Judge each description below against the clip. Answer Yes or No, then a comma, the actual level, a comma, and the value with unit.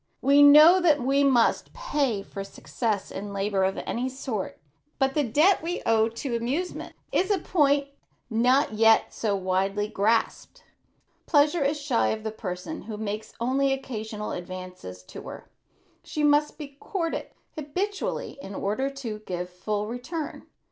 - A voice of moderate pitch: No, high, 245 Hz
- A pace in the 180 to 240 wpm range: No, average, 155 wpm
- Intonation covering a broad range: Yes, wide, 5.7 semitones